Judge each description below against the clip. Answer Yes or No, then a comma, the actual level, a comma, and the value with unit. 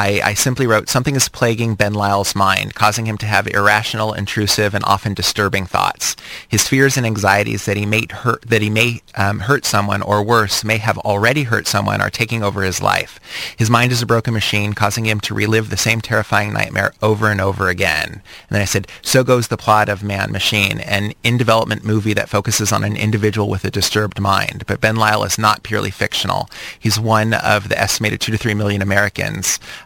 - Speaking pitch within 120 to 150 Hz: No, low, 105 Hz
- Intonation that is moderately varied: No, narrow, 2.0 semitones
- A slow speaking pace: No, fast, 205 wpm